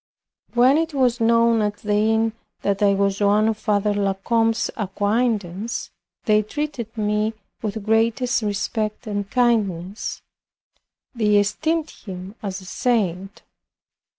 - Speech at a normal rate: No, slow, 125 wpm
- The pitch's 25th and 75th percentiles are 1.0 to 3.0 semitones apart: Yes, narrow, 2.4 semitones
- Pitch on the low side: No, high, 215 Hz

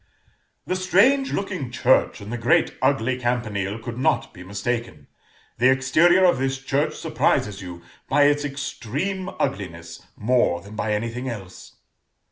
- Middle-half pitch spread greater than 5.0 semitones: Yes, wide, 5.5 semitones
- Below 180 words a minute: Yes, average, 140 wpm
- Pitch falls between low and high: No, low, 125 Hz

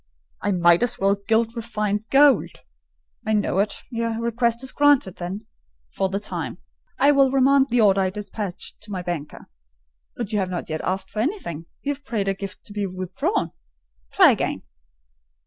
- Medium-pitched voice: No, high, 210 Hz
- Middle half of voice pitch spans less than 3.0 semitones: No, average, 3.9 semitones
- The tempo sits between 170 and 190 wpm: Yes, average, 175 wpm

